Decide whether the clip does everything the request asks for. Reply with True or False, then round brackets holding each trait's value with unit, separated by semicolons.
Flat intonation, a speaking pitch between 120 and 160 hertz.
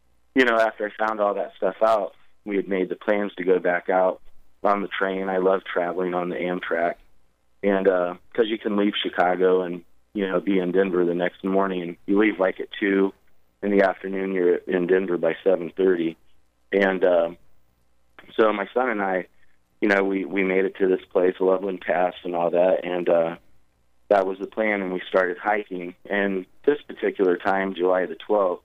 False (1.9 semitones; 95 Hz)